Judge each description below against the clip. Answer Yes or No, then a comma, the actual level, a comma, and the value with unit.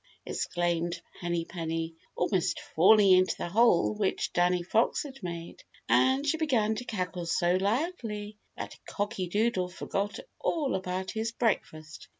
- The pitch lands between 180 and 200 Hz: Yes, high, 190 Hz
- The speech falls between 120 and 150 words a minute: Yes, average, 140 wpm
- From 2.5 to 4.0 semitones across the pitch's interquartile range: No, average, 4.4 semitones